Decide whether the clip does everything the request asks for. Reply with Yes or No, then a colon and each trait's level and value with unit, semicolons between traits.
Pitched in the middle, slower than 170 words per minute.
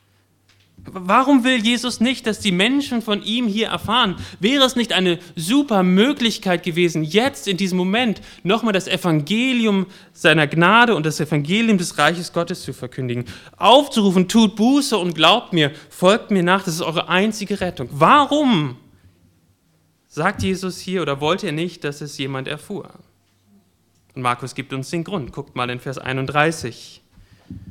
Yes: medium, 175 Hz; average, 155 wpm